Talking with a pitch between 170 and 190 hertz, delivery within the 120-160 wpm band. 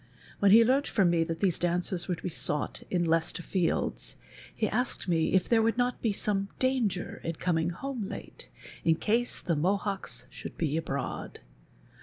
No: medium, 185 Hz; average, 180 wpm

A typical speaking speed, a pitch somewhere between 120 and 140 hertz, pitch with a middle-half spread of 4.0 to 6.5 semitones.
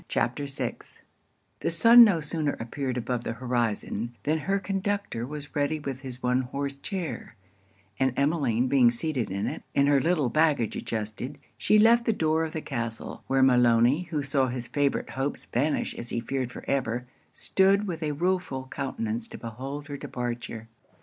Yes: average, 170 wpm; low, 135 Hz; average, 4.4 semitones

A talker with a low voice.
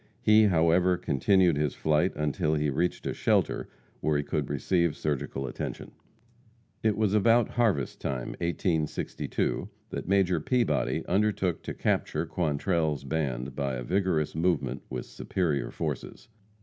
Yes: very low, 80 Hz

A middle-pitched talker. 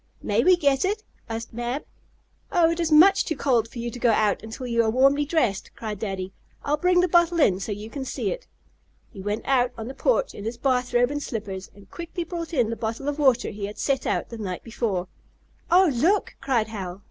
No: high, 245 Hz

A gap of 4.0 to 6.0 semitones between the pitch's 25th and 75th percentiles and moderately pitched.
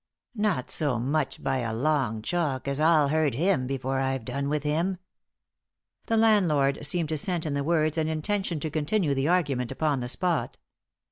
No: average, 3.6 semitones; medium, 150 Hz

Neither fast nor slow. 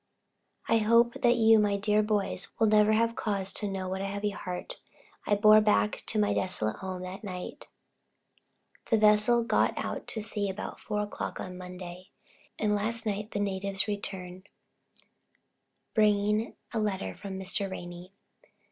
Yes: average, 155 wpm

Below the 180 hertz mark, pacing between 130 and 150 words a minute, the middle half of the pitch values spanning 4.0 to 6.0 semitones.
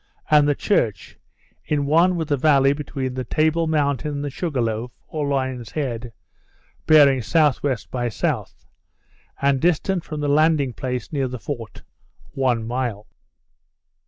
No: medium, 140 Hz; average, 145 wpm; average, 3.2 semitones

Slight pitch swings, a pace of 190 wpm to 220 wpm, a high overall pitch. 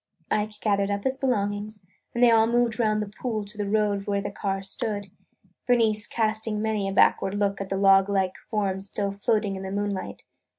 Yes: narrow, 1.6 semitones; average, 200 wpm; high, 205 Hz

